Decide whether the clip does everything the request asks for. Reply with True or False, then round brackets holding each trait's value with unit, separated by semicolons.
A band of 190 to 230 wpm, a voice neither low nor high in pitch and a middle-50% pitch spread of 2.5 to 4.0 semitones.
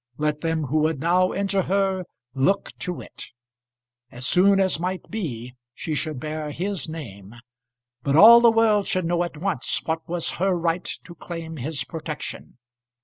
False (165 wpm; 165 Hz; 3.7 semitones)